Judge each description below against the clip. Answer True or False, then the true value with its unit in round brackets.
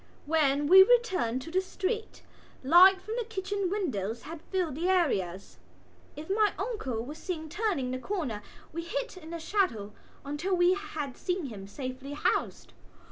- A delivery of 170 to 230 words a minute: False (160 wpm)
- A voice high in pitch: True (335 Hz)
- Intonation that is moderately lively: False (6.1 semitones)